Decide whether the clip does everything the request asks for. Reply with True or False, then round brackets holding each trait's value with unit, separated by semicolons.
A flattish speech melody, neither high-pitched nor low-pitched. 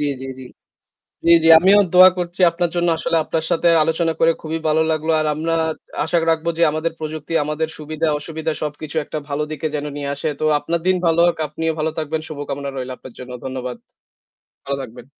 True (2.2 semitones; 155 Hz)